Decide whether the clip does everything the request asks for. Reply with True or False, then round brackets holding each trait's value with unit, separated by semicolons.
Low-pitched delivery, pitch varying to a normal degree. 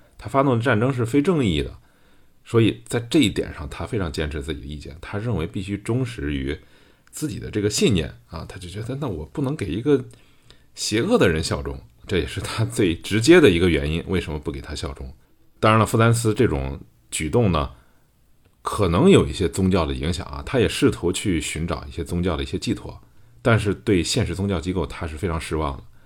False (90 Hz; 6.4 semitones)